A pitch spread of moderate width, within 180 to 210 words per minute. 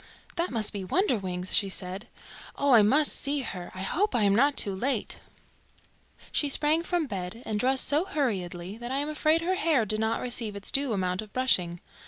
No: wide, 6.6 semitones; average, 200 wpm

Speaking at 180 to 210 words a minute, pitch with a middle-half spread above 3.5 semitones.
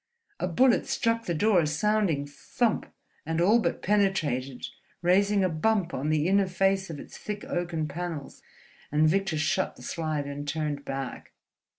No: average, 165 wpm; average, 4.7 semitones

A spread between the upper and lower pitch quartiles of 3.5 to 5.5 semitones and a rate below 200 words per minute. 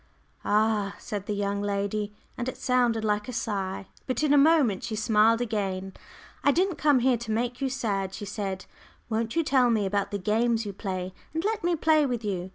No: average, 3.8 semitones; fast, 205 wpm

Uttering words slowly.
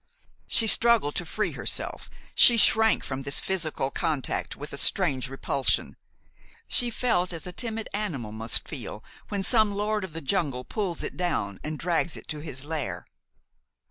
No: average, 165 wpm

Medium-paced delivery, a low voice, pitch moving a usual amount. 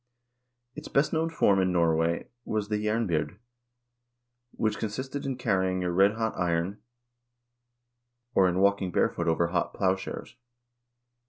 No: slow, 130 wpm; low, 100 Hz; average, 3.8 semitones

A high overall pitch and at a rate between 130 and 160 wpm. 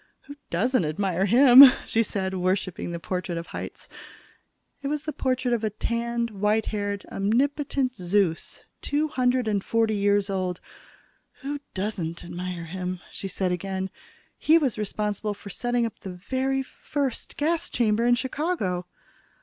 Yes: high, 210 Hz; average, 150 wpm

